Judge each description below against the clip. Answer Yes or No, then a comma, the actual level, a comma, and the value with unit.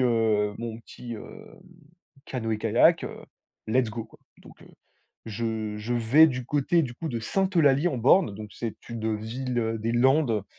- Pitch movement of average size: Yes, average, 3.1 semitones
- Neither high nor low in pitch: No, low, 115 Hz